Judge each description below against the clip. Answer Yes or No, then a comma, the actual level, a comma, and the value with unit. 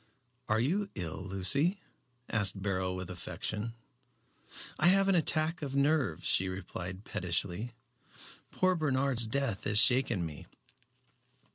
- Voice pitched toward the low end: Yes, low, 115 Hz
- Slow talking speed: Yes, slow, 120 wpm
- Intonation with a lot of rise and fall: Yes, wide, 7.7 semitones